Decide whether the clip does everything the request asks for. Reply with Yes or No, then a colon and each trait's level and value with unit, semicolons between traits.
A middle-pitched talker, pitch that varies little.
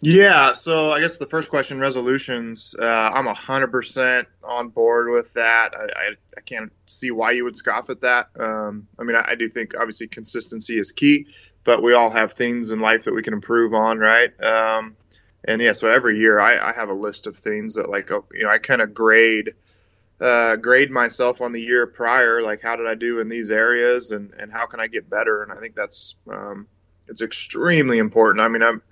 No: low, 115 Hz; narrow, 1.9 semitones